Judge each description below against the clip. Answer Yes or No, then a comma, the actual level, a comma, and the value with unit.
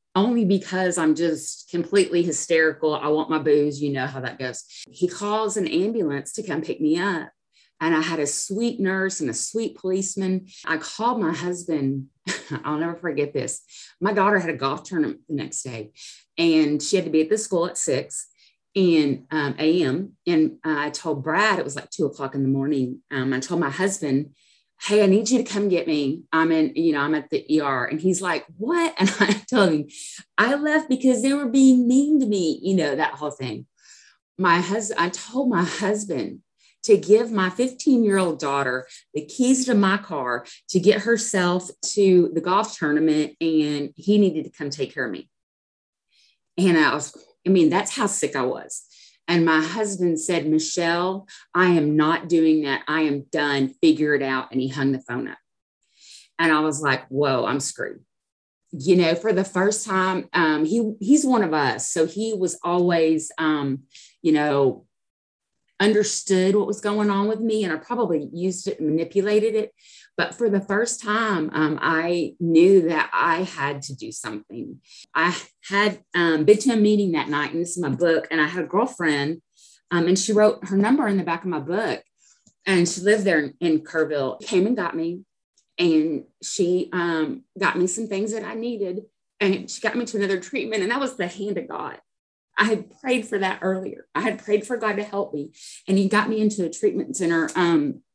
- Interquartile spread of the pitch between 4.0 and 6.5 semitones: Yes, average, 5.1 semitones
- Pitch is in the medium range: Yes, medium, 180 Hz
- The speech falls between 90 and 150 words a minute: No, average, 200 wpm